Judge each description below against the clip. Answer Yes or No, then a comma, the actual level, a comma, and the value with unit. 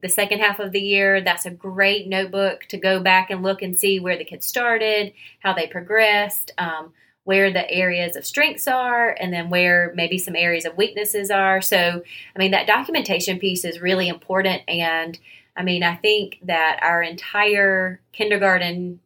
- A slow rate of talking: No, average, 185 wpm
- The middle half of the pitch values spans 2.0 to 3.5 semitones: Yes, narrow, 2.4 semitones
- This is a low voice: No, high, 190 Hz